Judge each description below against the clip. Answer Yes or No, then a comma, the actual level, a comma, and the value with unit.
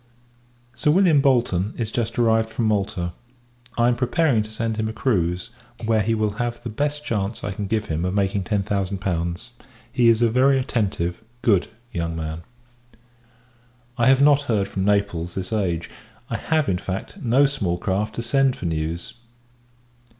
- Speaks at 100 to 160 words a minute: No, average, 175 wpm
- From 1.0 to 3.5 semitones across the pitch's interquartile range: No, average, 4.3 semitones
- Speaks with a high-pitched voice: No, low, 110 Hz